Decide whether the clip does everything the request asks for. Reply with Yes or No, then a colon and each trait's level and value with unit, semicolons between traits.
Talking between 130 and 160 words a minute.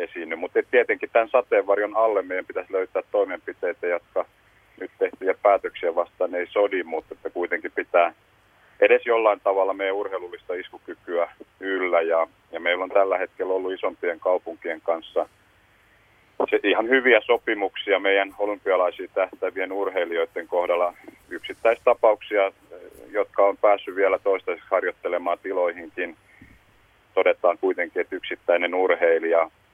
No: average, 120 wpm